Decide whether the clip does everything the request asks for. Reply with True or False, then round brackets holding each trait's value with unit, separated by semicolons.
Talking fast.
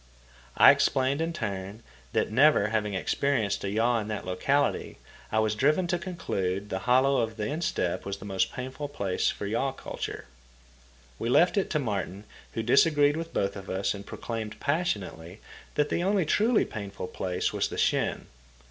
False (175 wpm)